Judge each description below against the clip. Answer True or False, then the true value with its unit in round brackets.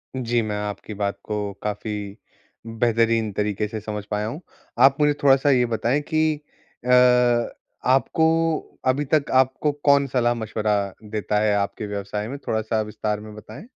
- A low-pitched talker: True (110 Hz)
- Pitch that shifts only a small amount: False (4.2 semitones)